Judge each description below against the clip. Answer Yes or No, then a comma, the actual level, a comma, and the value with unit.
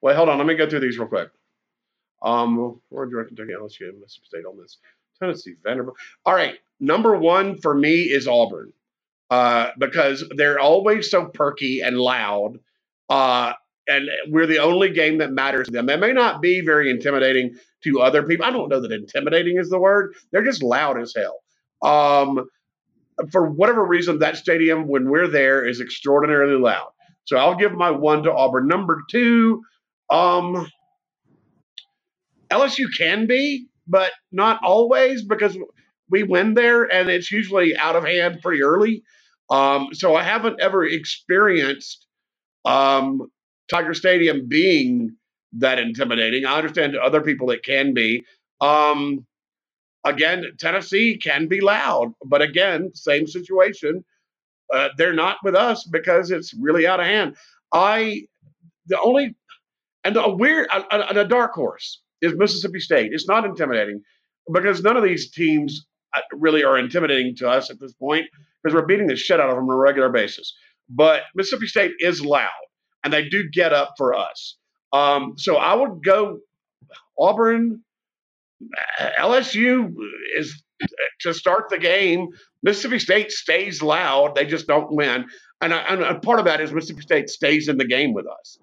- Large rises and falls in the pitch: Yes, wide, 6.3 semitones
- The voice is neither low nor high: Yes, medium, 165 Hz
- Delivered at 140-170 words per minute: Yes, average, 160 wpm